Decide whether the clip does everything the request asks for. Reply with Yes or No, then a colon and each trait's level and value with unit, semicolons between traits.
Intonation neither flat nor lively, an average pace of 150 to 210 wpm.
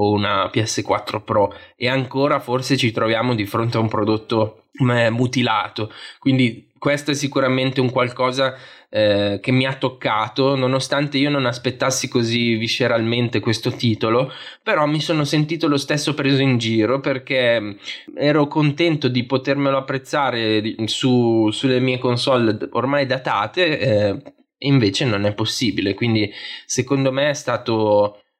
No: average, 3.4 semitones; average, 135 wpm